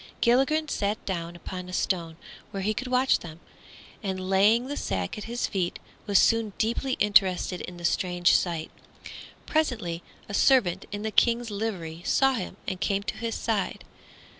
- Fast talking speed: No, average, 165 wpm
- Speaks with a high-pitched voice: Yes, high, 200 Hz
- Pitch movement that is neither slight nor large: Yes, average, 4.5 semitones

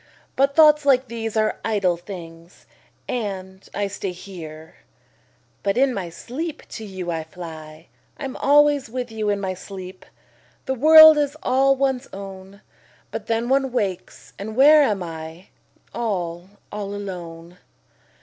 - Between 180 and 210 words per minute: No, average, 145 wpm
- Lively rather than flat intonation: Yes, wide, 6.5 semitones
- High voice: Yes, high, 205 Hz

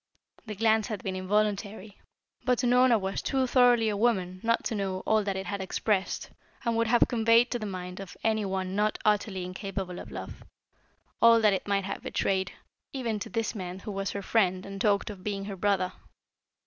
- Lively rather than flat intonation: No, average, 2.8 semitones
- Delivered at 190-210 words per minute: Yes, average, 200 wpm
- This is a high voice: Yes, high, 205 Hz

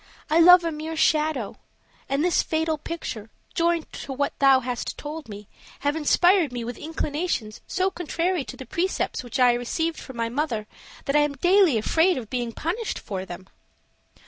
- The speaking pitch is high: Yes, very high, 295 Hz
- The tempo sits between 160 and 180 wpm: Yes, average, 175 wpm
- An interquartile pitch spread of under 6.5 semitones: Yes, wide, 5.4 semitones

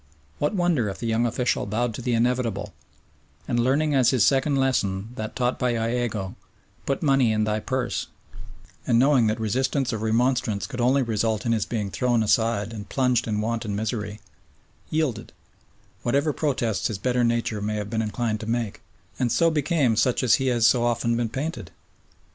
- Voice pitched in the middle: No, low, 120 Hz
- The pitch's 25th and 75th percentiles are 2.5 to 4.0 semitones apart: Yes, average, 2.9 semitones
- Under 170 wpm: No, average, 185 wpm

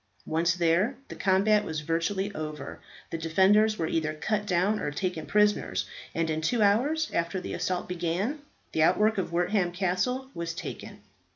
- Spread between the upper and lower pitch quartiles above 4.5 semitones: No, average, 4.1 semitones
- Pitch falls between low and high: Yes, medium, 180 Hz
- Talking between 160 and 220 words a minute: Yes, average, 165 wpm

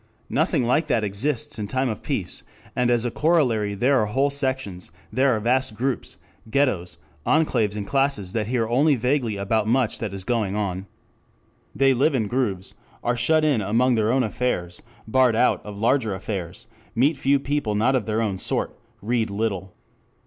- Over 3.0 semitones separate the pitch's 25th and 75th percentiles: Yes, average, 4.1 semitones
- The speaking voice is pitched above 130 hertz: No, low, 115 Hz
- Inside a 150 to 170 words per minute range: No, average, 180 wpm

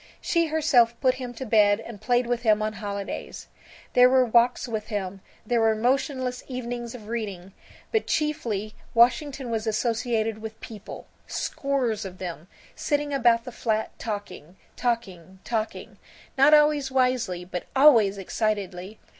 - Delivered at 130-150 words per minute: Yes, average, 145 wpm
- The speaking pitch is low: No, high, 230 Hz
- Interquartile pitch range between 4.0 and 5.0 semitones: No, average, 3.3 semitones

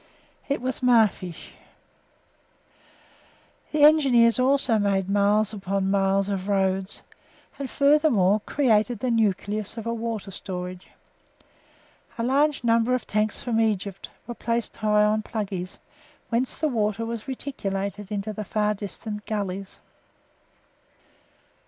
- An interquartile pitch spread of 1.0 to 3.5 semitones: Yes, average, 3.1 semitones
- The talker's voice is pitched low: No, high, 215 Hz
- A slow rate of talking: Yes, slow, 120 wpm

